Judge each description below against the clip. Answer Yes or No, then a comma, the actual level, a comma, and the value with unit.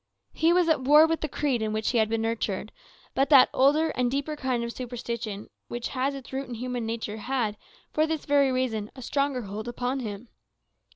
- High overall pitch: Yes, very high, 250 Hz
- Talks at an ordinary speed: No, fast, 210 wpm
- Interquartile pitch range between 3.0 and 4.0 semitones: Yes, average, 3.6 semitones